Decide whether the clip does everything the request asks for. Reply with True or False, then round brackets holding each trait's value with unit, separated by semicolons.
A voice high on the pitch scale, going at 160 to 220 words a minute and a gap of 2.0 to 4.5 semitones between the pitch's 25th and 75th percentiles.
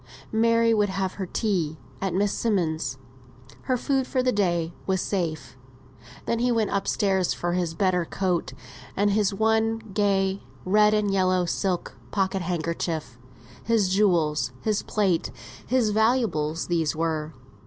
False (195 Hz; 145 wpm; 3.9 semitones)